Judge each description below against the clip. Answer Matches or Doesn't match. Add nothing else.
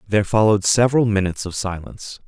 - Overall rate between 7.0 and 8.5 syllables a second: Matches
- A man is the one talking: Matches